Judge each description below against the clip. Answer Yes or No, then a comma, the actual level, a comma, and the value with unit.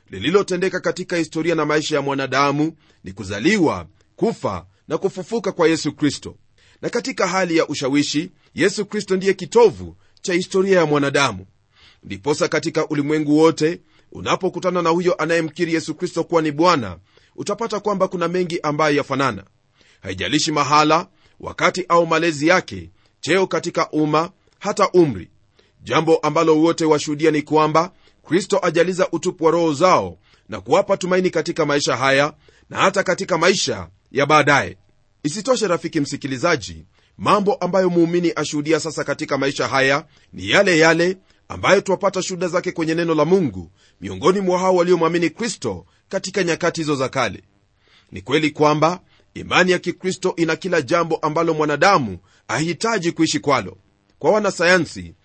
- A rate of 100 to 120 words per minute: No, fast, 140 wpm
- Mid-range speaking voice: Yes, medium, 160 Hz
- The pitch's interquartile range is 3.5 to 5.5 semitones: Yes, average, 4.1 semitones